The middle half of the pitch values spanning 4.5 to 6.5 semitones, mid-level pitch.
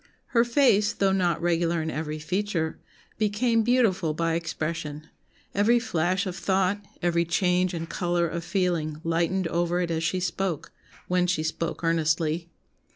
No: average, 2.7 semitones; medium, 175 Hz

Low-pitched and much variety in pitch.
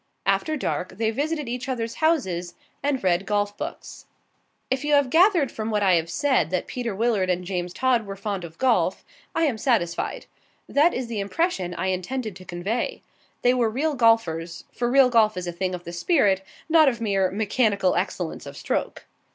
No: high, 220 Hz; wide, 6.0 semitones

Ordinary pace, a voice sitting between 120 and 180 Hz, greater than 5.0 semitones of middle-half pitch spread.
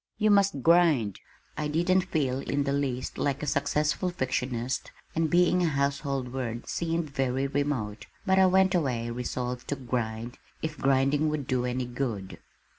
No: average, 160 wpm; medium, 140 Hz; average, 4.3 semitones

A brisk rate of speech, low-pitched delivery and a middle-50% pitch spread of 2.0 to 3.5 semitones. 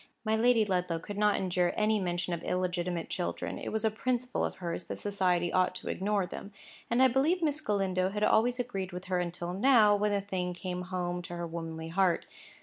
No: fast, 210 wpm; medium, 185 Hz; average, 3.2 semitones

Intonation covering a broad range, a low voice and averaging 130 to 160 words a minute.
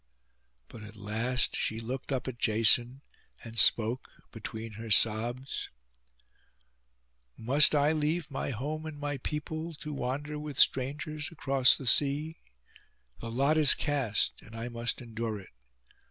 No: average, 4.4 semitones; low, 130 Hz; average, 140 wpm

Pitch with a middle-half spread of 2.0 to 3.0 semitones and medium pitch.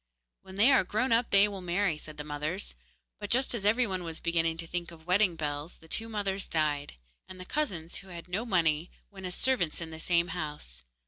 No: average, 3.9 semitones; medium, 180 Hz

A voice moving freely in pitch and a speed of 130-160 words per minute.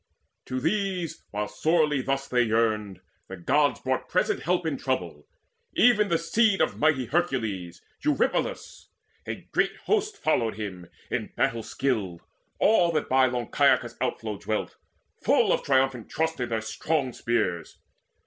Yes: wide, 6.9 semitones; average, 145 wpm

